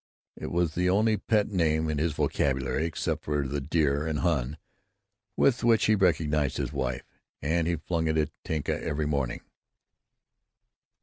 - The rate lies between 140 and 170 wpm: Yes, average, 150 wpm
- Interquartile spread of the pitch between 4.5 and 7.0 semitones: No, average, 3.1 semitones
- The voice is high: No, very low, 80 Hz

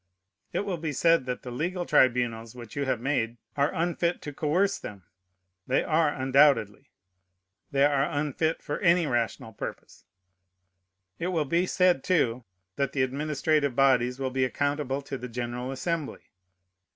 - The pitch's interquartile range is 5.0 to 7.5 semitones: No, average, 4.0 semitones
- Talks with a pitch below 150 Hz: Yes, medium, 140 Hz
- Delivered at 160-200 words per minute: No, average, 150 wpm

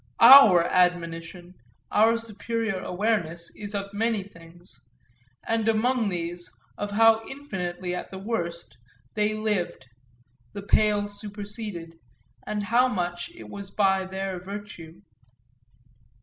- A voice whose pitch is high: Yes, high, 200 Hz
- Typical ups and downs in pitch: Yes, average, 3.5 semitones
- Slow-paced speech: Yes, slow, 115 wpm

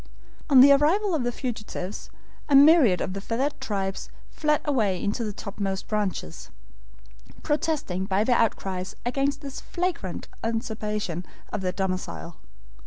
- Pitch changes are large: Yes, wide, 6.4 semitones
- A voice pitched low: No, high, 220 Hz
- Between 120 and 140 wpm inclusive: Yes, slow, 135 wpm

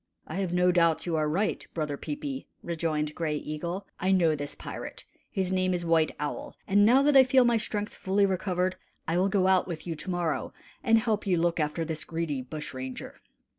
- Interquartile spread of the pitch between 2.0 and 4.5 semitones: Yes, average, 3.8 semitones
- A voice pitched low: No, medium, 175 Hz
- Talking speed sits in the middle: No, fast, 210 wpm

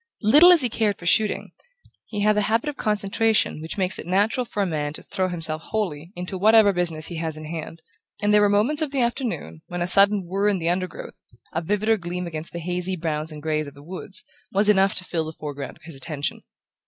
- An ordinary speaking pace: No, fast, 230 wpm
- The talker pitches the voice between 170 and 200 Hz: Yes, medium, 185 Hz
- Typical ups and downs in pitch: Yes, average, 4.5 semitones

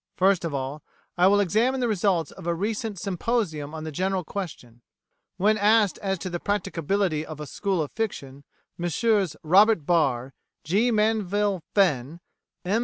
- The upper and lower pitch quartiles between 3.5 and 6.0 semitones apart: Yes, average, 4.7 semitones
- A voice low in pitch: No, medium, 185 Hz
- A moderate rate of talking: Yes, average, 160 wpm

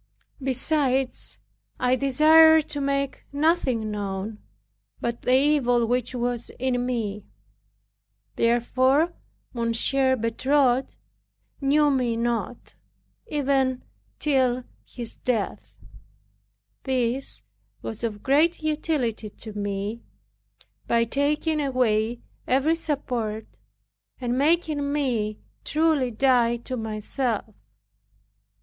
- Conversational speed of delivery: No, slow, 90 wpm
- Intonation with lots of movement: No, average, 3.5 semitones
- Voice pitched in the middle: No, very high, 255 Hz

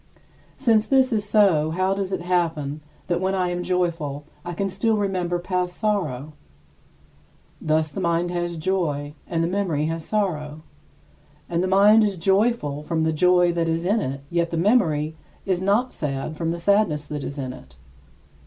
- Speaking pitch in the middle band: Yes, medium, 175 Hz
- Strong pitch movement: No, average, 3.8 semitones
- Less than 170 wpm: No, average, 175 wpm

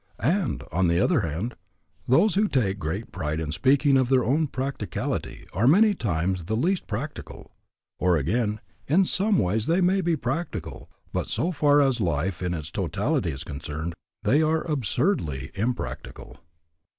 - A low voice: Yes, low, 120 Hz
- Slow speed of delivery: No, average, 160 wpm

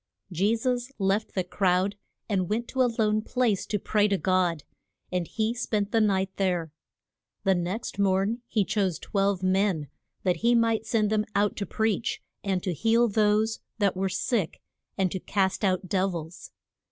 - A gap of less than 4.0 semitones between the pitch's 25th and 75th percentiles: Yes, average, 2.8 semitones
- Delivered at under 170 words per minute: No, average, 175 wpm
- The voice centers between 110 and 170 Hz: No, high, 200 Hz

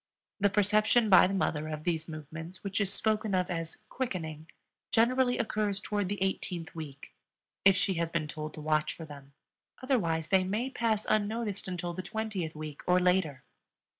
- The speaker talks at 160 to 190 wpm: Yes, average, 170 wpm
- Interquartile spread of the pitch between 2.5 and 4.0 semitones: No, average, 4.8 semitones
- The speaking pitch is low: No, medium, 185 Hz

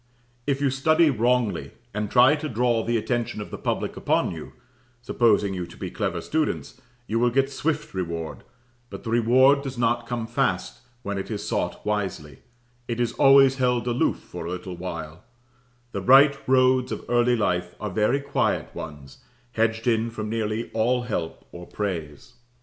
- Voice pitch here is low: Yes, low, 115 Hz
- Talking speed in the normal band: Yes, average, 170 wpm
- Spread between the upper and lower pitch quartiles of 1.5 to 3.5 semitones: No, average, 4.2 semitones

